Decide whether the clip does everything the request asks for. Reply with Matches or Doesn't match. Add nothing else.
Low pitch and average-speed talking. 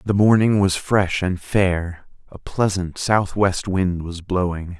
Matches